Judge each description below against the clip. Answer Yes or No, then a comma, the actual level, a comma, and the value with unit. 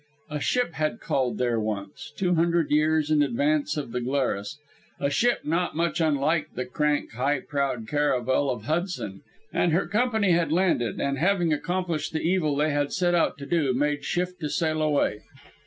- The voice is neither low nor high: Yes, medium, 150 Hz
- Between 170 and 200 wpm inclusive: Yes, average, 180 wpm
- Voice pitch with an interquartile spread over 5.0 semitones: No, average, 4.0 semitones